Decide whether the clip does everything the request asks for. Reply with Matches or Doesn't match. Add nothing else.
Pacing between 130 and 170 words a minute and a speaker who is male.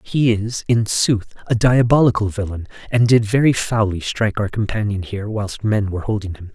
Doesn't match